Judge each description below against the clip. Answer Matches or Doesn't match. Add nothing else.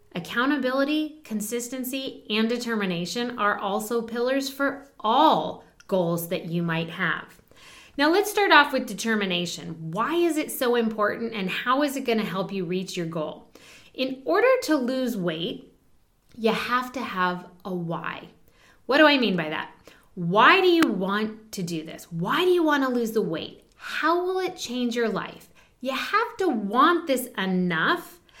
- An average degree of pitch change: Doesn't match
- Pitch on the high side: Matches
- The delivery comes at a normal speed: Matches